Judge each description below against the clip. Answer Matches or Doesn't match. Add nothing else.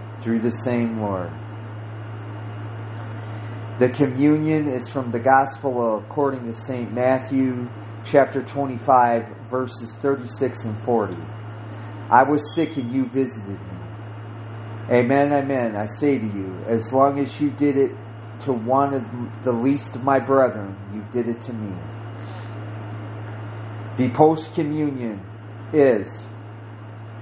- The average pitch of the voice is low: Matches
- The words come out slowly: Matches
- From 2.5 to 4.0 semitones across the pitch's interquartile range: Matches